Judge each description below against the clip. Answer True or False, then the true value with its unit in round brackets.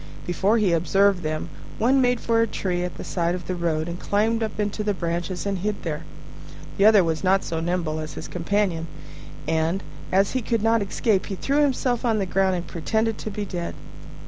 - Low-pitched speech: False (195 Hz)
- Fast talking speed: True (210 wpm)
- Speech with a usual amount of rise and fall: True (4.0 semitones)